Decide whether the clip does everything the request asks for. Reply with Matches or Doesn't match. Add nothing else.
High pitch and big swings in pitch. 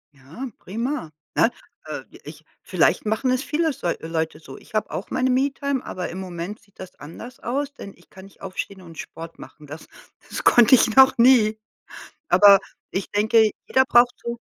Matches